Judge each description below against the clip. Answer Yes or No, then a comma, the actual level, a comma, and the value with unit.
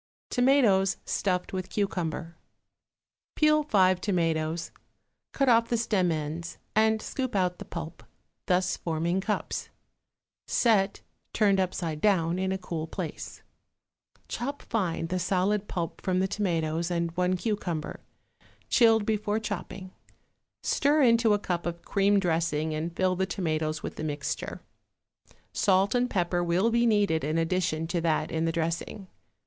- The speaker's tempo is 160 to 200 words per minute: No, average, 140 wpm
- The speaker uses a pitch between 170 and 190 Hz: Yes, medium, 185 Hz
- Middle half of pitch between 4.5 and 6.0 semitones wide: No, average, 3.8 semitones